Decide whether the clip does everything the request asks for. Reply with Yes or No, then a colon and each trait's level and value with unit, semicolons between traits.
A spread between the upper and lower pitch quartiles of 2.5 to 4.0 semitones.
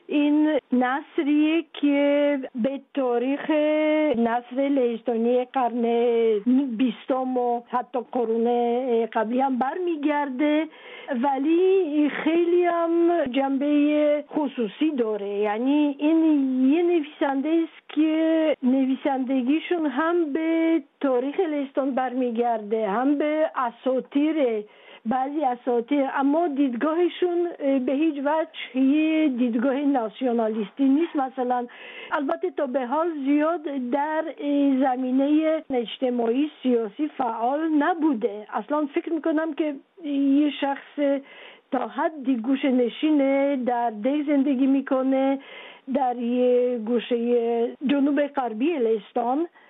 Yes: average, 3.6 semitones